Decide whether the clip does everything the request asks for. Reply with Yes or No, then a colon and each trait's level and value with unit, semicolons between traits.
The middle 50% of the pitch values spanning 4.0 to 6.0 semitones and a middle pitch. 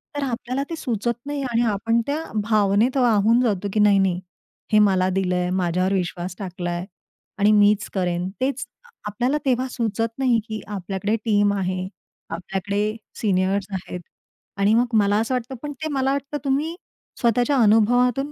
No: average, 4.4 semitones; high, 210 Hz